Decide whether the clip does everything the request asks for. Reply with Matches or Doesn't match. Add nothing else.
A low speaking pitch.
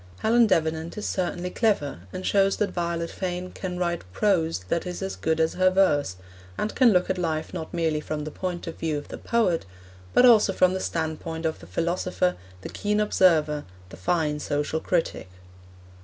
Doesn't match